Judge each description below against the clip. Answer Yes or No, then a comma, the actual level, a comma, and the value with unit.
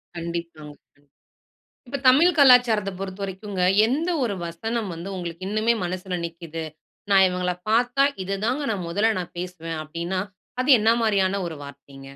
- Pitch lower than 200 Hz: Yes, high, 190 Hz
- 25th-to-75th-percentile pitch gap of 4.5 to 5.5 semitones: Yes, average, 4.9 semitones